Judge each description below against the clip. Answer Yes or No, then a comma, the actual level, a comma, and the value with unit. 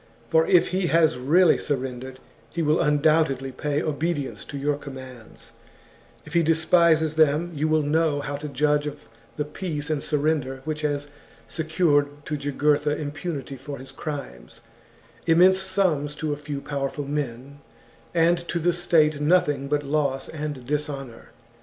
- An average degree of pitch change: No, narrow, 2.2 semitones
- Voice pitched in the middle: Yes, medium, 150 Hz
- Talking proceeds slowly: No, average, 150 wpm